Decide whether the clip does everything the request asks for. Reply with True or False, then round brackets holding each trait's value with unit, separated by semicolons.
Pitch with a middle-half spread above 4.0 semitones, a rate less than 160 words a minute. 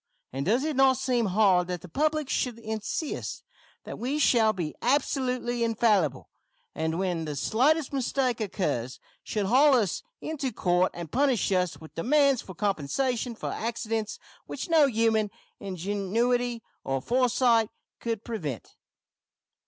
True (5.5 semitones; 135 wpm)